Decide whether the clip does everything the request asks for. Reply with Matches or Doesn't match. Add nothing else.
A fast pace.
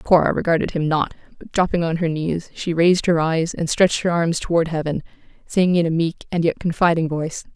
Matches